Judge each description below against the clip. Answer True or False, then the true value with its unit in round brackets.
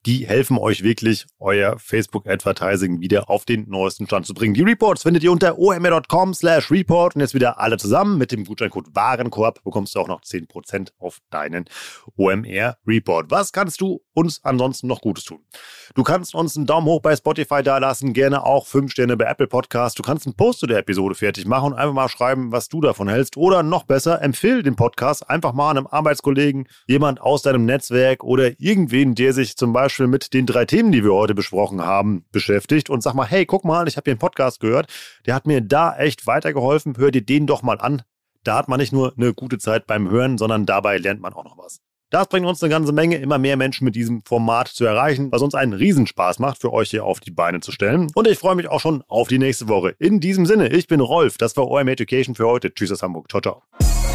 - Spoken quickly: True (225 wpm)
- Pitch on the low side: True (130 Hz)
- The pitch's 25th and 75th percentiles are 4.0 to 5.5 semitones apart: True (5.0 semitones)